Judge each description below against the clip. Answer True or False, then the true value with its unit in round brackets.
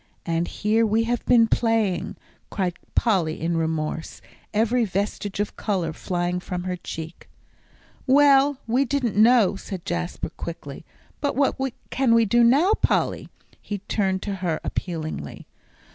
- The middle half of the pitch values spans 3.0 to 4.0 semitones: False (5.0 semitones)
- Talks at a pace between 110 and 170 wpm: True (140 wpm)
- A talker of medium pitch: False (205 Hz)